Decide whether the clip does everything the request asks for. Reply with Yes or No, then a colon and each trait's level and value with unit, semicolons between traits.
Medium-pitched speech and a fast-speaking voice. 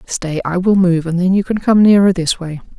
Yes: medium, 180 Hz; fast, 260 wpm